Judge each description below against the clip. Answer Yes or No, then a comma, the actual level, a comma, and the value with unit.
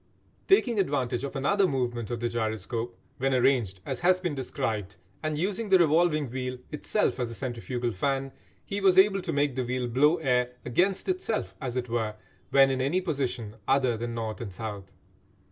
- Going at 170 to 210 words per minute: Yes, average, 180 wpm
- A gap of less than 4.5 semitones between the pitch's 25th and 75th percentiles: No, average, 5.2 semitones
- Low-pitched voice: Yes, low, 130 Hz